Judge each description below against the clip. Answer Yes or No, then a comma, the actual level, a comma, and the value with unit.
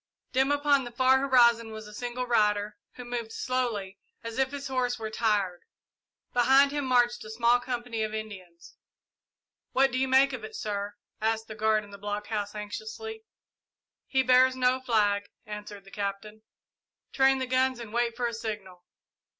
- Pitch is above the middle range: Yes, high, 235 Hz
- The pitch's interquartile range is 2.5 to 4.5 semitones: Yes, average, 3.5 semitones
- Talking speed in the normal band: Yes, average, 170 wpm